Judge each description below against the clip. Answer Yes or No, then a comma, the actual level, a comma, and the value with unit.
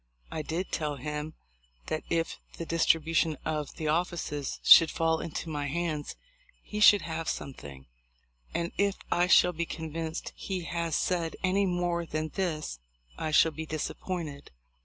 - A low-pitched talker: No, medium, 165 Hz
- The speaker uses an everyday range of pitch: No, narrow, 2.0 semitones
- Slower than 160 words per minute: Yes, average, 150 wpm